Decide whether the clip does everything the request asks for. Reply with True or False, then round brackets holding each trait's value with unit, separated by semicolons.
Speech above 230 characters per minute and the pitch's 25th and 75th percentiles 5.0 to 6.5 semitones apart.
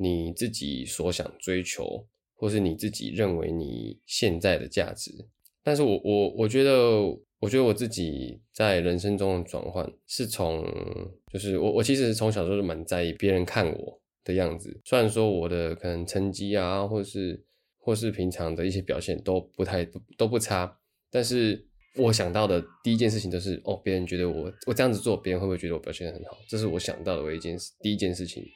False (300 characters per minute; 3.4 semitones)